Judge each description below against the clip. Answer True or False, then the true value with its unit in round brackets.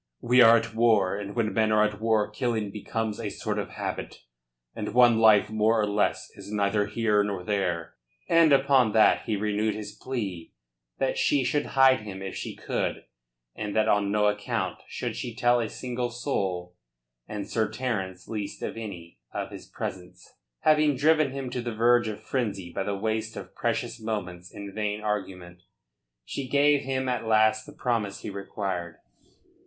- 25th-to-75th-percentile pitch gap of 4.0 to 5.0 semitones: False (3.1 semitones)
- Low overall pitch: True (110 Hz)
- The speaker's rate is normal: True (180 wpm)